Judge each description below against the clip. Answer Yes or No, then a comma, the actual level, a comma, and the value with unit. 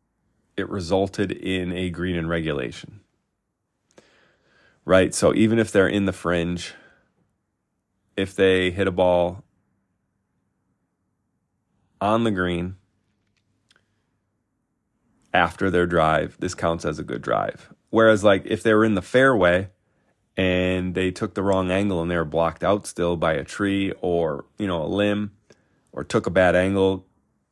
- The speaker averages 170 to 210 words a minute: No, average, 140 wpm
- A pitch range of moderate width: No, narrow, 2.3 semitones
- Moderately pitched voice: No, very low, 95 Hz